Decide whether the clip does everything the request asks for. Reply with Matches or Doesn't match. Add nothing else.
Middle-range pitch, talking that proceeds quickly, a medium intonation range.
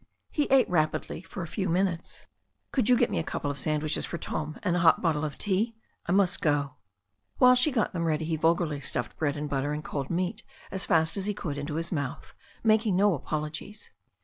Matches